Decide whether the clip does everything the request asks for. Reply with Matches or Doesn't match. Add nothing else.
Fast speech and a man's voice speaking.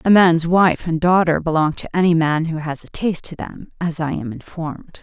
Doesn't match